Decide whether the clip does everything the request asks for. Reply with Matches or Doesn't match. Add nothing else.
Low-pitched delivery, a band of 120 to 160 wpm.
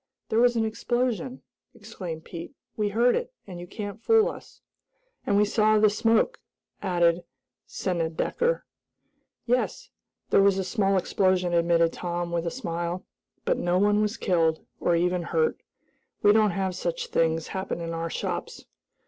Doesn't match